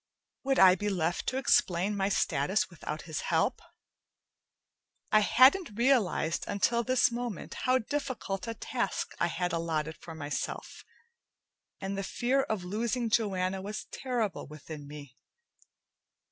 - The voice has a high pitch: Yes, high, 195 Hz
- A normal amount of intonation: No, wide, 5.8 semitones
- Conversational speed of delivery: No, slow, 130 wpm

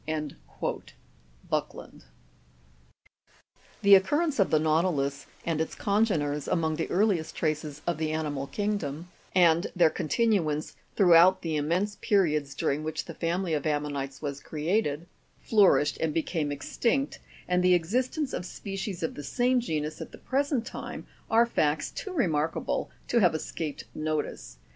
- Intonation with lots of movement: No, average, 4.9 semitones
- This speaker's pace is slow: No, average, 145 wpm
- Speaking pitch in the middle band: Yes, medium, 165 Hz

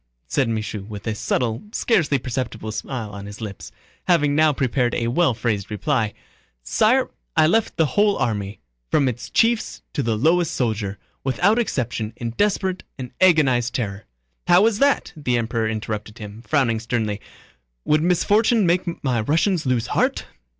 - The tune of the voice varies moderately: No, wide, 7.0 semitones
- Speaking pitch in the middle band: No, low, 125 Hz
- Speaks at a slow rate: No, average, 155 wpm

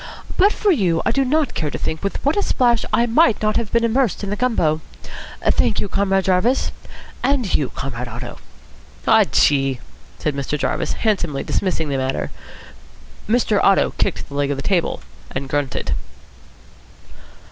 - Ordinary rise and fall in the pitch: No, wide, 8.6 semitones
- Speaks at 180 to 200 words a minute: No, average, 170 wpm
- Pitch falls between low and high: No, high, 195 Hz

